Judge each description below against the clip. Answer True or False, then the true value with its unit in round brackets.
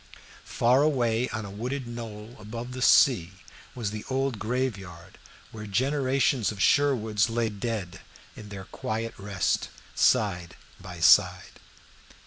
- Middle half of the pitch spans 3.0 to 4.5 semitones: True (3.8 semitones)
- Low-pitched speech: True (110 Hz)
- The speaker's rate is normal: False (125 wpm)